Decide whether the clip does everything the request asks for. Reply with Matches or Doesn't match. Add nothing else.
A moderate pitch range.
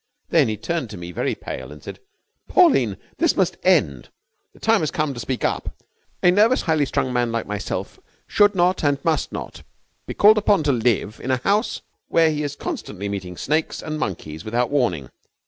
Doesn't match